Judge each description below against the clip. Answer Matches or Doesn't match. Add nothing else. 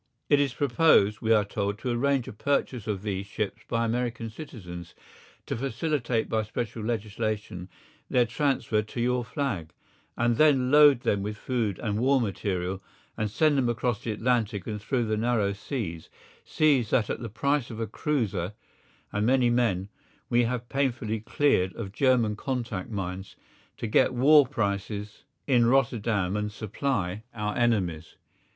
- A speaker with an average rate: Matches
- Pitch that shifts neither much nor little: Matches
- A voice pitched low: Matches